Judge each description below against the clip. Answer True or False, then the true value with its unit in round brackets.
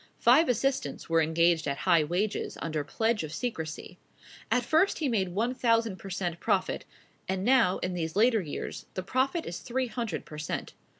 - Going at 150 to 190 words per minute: True (180 wpm)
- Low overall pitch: False (195 Hz)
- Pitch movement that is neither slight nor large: False (6.4 semitones)